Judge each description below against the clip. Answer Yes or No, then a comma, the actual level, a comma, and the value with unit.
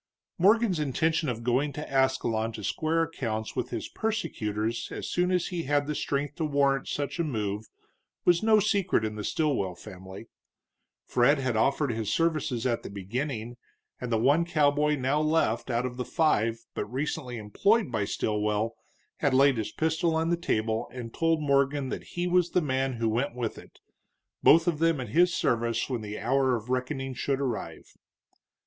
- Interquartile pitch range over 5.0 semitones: Yes, wide, 5.6 semitones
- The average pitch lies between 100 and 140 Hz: Yes, low, 135 Hz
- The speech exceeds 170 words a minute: Yes, average, 180 wpm